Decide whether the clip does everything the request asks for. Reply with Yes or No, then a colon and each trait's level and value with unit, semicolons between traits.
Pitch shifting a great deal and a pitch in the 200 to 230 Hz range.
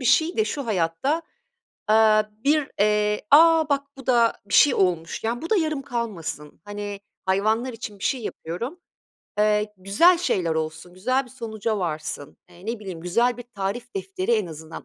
Yes: wide, 6.1 semitones; high, 220 Hz